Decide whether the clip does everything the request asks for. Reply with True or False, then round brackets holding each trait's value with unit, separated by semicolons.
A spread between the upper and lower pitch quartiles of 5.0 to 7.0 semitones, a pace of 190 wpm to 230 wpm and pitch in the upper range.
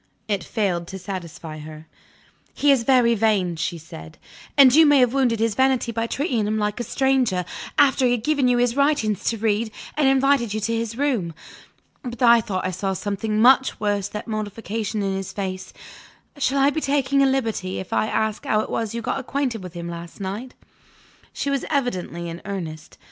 True (5.3 semitones; 195 wpm; 220 Hz)